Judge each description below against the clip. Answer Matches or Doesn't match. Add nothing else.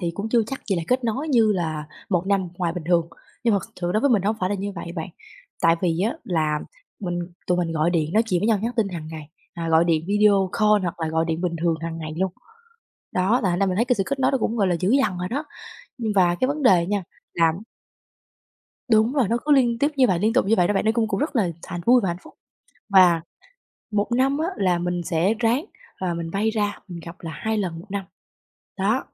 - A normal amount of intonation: Matches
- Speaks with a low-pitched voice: Doesn't match